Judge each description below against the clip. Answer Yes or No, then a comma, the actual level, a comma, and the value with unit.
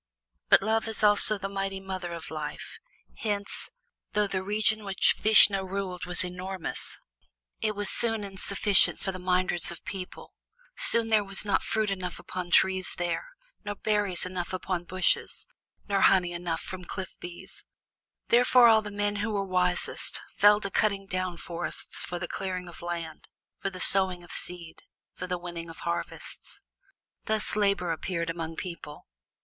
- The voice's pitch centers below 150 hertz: No, high, 190 Hz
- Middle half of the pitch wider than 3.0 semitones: No, narrow, 2.6 semitones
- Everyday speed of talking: Yes, average, 160 wpm